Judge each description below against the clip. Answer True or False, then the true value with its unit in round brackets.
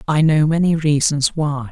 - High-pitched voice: False (150 Hz)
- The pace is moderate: True (175 wpm)